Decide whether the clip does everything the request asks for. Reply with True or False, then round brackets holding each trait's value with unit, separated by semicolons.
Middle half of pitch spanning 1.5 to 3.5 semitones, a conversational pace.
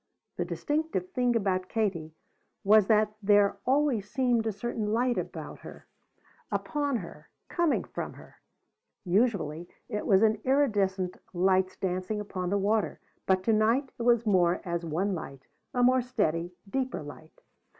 False (4.5 semitones; 150 wpm)